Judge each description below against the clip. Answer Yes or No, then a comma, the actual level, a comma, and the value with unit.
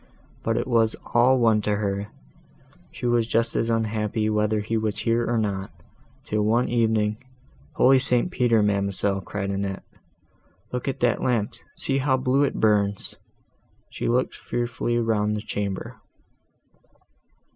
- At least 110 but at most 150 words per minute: Yes, average, 145 wpm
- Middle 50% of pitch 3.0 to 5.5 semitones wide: No, narrow, 2.5 semitones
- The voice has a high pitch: No, low, 110 Hz